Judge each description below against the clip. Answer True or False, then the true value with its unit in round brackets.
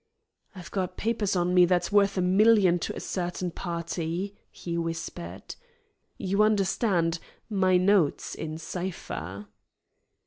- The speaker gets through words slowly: True (125 wpm)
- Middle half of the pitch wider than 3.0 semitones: False (2.6 semitones)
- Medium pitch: True (180 Hz)